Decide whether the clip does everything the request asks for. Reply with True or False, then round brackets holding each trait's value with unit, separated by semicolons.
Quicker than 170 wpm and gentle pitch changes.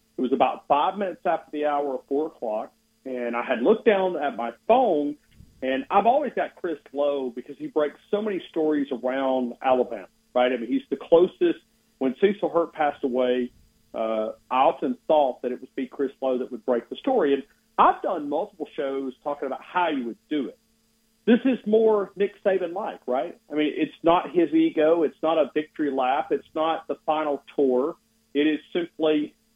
False (195 wpm; 4.5 semitones)